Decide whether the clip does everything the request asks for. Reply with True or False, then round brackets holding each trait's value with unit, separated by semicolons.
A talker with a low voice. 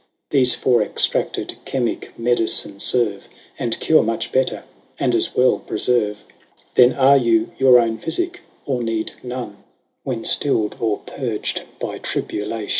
True (120 Hz)